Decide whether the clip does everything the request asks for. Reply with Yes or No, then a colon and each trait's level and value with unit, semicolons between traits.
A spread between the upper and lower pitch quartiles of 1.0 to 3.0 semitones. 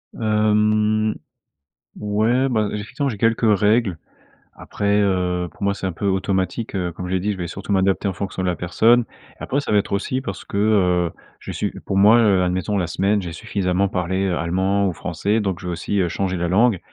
Yes: average, 2.7 semitones